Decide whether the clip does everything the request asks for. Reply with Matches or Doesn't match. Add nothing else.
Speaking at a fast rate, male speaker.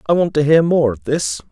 Matches